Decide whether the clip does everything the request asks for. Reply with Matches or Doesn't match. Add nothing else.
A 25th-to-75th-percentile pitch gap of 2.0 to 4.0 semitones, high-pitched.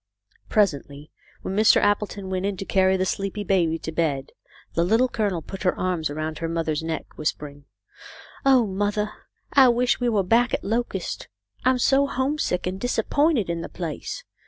Doesn't match